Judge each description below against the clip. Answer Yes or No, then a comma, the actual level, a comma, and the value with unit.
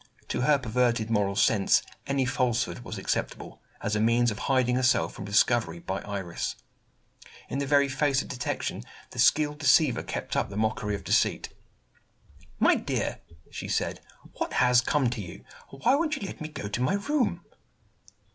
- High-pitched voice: No, low, 125 Hz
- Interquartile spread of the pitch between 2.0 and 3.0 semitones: No, average, 4.8 semitones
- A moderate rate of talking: Yes, average, 170 wpm